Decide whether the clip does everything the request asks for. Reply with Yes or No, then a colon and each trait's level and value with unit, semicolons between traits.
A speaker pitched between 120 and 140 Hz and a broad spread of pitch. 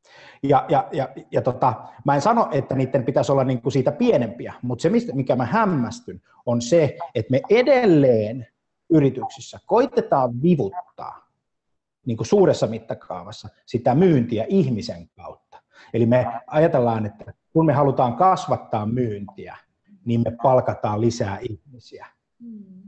Yes: low, 130 Hz; wide, 5.9 semitones